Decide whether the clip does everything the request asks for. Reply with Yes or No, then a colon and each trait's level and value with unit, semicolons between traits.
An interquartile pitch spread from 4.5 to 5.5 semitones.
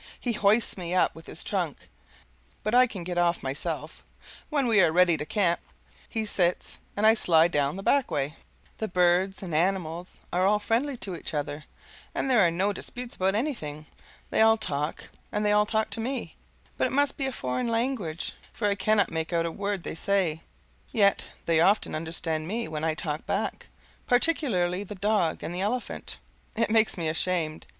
Yes: average, 4.8 semitones